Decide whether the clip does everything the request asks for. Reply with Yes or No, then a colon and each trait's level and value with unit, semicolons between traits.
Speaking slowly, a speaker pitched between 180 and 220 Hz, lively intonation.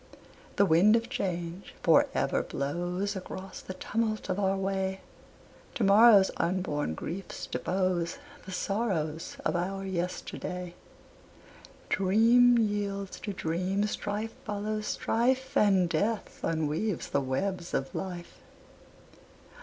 No: slow, 115 wpm; high, 190 Hz; average, 2.9 semitones